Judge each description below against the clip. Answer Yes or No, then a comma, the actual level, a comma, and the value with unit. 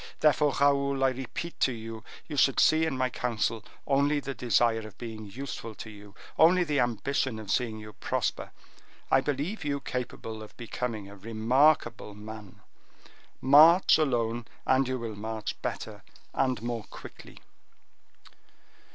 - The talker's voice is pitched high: No, low, 125 Hz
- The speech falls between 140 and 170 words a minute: Yes, average, 145 wpm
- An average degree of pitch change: Yes, average, 4.1 semitones